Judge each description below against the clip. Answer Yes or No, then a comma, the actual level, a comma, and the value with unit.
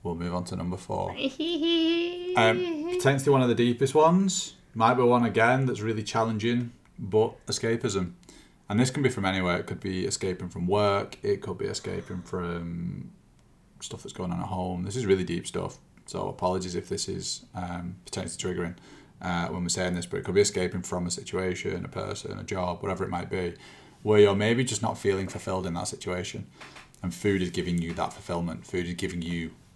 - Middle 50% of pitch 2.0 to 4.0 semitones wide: No, average, 5.0 semitones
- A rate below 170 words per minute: No, average, 200 wpm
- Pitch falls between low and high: No, very low, 95 Hz